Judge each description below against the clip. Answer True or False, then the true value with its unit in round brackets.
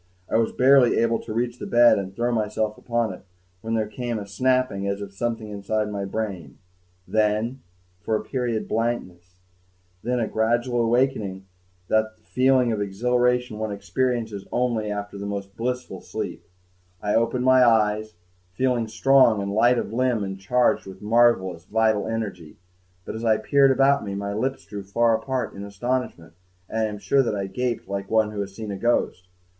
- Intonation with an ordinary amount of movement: True (3.1 semitones)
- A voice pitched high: False (110 Hz)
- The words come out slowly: False (180 wpm)